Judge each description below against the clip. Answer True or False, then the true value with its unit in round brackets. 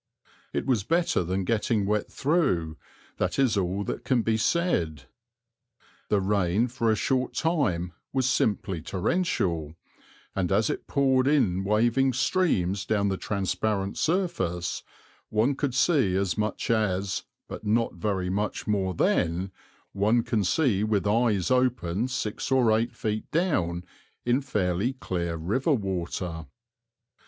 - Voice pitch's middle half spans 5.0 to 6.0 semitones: True (5.6 semitones)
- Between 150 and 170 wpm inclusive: False (135 wpm)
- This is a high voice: False (105 Hz)